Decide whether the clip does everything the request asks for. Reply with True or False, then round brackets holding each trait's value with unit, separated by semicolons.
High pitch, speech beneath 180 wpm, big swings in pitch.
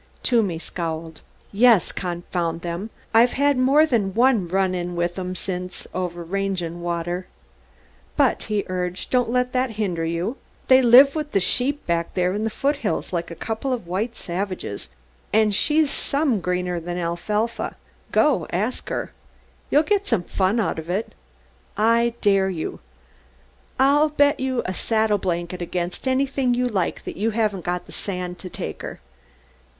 True (195 Hz; 165 wpm; 5.8 semitones)